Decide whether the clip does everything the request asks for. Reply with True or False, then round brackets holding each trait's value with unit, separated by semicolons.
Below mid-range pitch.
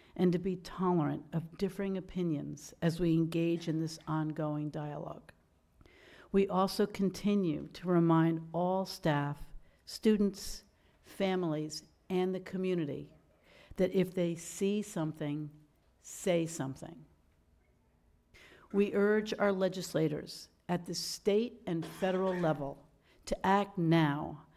False (170 Hz)